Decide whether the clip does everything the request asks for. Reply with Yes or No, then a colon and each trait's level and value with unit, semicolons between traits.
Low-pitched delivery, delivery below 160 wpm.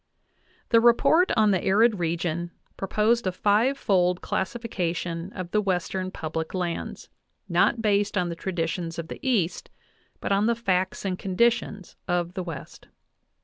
No: medium, 185 Hz; average, 145 wpm